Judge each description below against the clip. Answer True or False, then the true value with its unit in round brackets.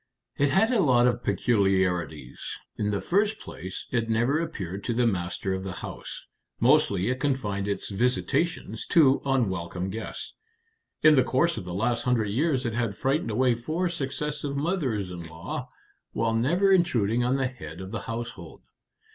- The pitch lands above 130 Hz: False (120 Hz)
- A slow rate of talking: False (165 wpm)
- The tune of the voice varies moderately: False (6.0 semitones)